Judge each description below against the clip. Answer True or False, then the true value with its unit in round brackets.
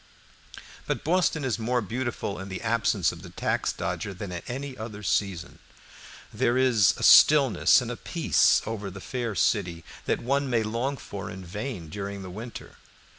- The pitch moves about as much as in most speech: True (4.3 semitones)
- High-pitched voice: False (110 Hz)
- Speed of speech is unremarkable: True (175 wpm)